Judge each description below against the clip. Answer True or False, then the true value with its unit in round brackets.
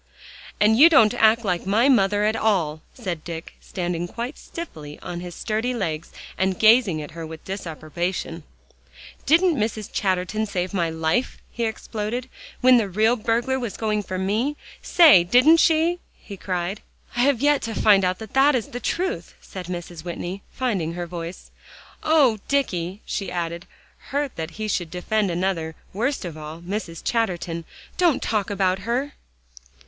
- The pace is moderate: True (160 wpm)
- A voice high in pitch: True (205 Hz)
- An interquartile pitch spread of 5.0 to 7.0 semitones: True (5.5 semitones)